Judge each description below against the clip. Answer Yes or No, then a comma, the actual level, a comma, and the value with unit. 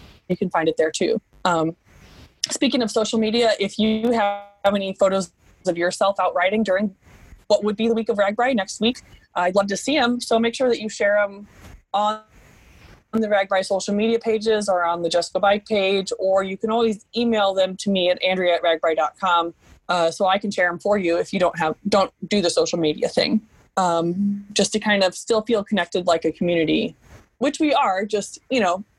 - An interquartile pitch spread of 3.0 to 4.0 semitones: Yes, average, 3.3 semitones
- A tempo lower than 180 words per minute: No, fast, 205 wpm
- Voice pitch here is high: Yes, high, 200 Hz